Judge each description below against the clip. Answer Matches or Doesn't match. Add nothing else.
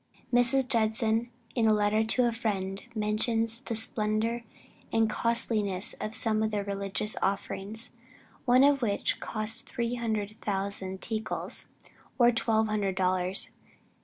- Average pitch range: Doesn't match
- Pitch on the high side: Matches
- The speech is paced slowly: Matches